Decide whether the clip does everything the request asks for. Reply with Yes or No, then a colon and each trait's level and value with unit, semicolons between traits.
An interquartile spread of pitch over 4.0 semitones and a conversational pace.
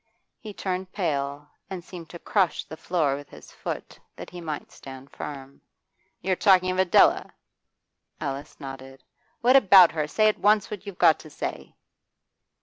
Yes: average, 5.0 semitones; average, 160 wpm